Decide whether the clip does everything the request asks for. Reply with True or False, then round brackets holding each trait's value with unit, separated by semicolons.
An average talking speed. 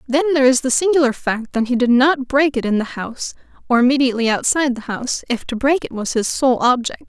False (235 wpm)